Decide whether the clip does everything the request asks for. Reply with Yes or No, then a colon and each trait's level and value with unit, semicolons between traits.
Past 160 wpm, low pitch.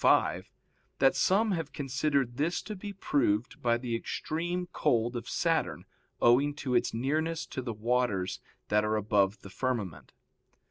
No: average, 155 wpm; low, 125 Hz